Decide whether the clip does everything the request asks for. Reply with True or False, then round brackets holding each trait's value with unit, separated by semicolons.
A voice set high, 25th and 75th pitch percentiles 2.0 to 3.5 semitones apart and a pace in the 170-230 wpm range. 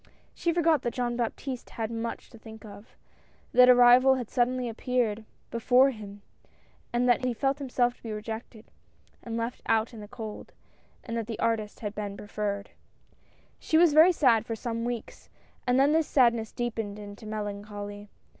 True (230 Hz; 2.7 semitones; 185 wpm)